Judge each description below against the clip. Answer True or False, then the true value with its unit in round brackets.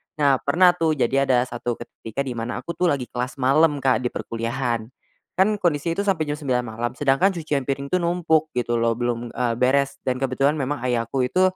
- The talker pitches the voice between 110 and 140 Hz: True (135 Hz)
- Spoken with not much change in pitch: False (4.1 semitones)